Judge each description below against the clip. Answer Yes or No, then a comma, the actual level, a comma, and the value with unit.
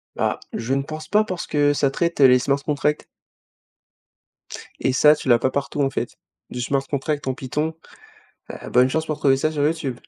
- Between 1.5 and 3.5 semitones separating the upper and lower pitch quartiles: Yes, narrow, 2.5 semitones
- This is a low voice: No, medium, 145 Hz